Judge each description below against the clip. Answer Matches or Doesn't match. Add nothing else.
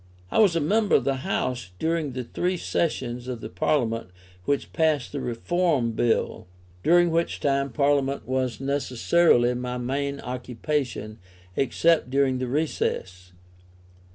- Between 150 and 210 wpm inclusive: Doesn't match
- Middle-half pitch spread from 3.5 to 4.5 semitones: Matches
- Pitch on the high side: Doesn't match